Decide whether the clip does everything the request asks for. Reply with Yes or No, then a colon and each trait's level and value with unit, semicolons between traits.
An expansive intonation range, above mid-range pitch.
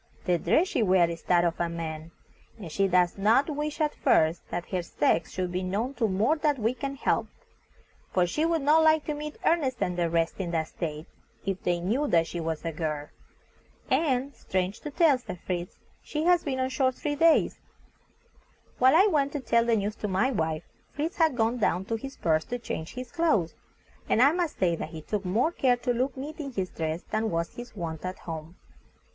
Yes: wide, 8.3 semitones; high, 220 Hz